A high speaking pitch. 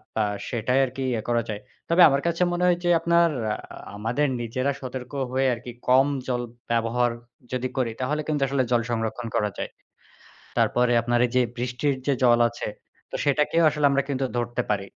No: low, 125 Hz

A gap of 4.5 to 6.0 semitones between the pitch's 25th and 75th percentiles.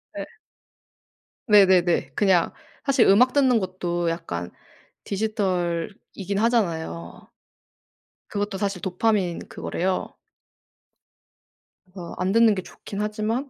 No: average, 3.4 semitones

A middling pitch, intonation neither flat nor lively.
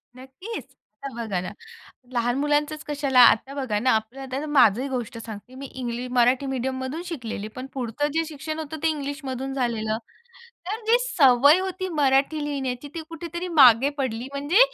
No: very high, 270 Hz; average, 3.6 semitones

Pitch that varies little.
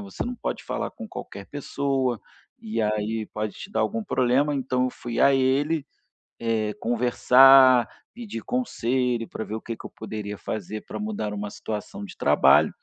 No: average, 4.6 semitones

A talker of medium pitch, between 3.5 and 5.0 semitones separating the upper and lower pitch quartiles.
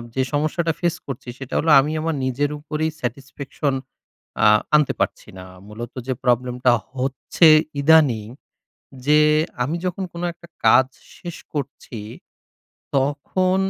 Yes: medium, 145 Hz; average, 3.8 semitones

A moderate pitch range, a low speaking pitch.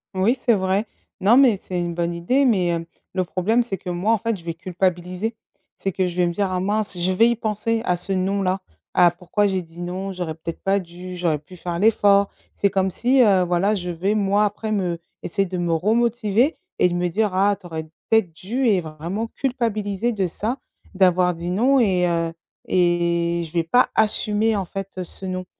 No: average, 3.3 semitones; high, 190 Hz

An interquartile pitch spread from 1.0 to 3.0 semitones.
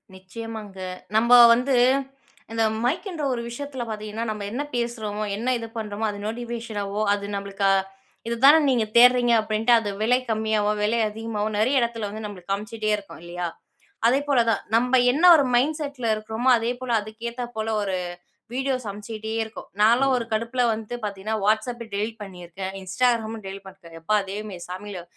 Yes: narrow, 2.6 semitones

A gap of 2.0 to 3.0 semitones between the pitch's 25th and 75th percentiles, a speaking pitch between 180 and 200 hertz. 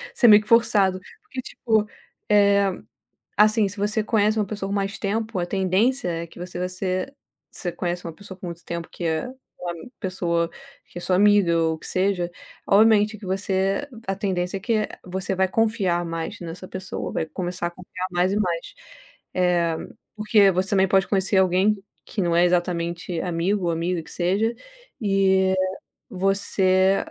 Yes: narrow, 2.6 semitones; high, 190 Hz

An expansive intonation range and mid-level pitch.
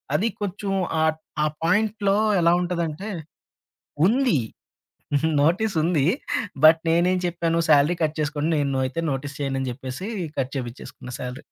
No: average, 4.4 semitones; medium, 160 Hz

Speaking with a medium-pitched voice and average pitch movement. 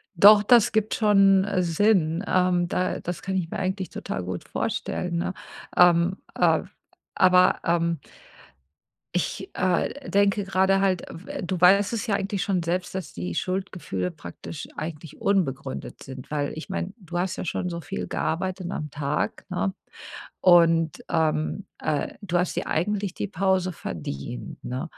Yes: medium, 180 Hz; average, 3.0 semitones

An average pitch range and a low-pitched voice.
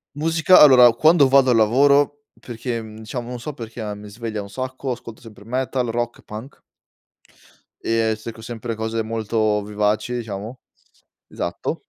Yes: average, 3.0 semitones; low, 115 Hz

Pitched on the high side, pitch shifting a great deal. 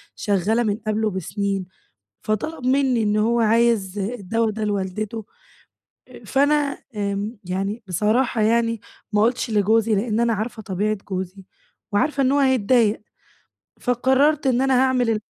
No: high, 220 Hz; average, 3.2 semitones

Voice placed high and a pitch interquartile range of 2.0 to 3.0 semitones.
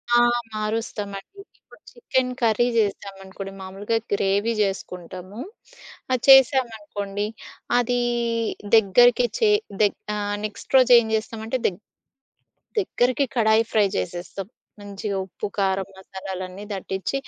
No: high, 210 Hz; average, 3.7 semitones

